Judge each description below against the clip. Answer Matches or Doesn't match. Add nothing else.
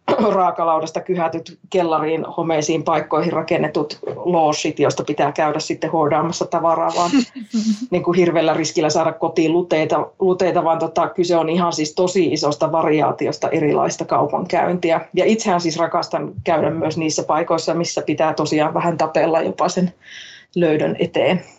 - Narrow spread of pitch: Matches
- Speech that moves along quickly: Doesn't match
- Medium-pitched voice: Matches